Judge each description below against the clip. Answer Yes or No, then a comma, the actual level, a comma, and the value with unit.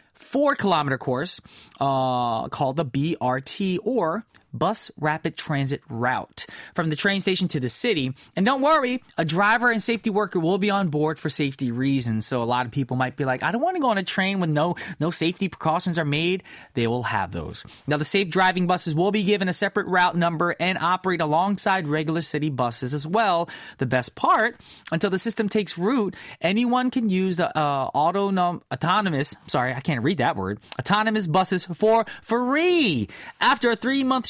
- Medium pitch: Yes, medium, 175 Hz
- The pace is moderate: Yes, average, 190 wpm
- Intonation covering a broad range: Yes, wide, 6.1 semitones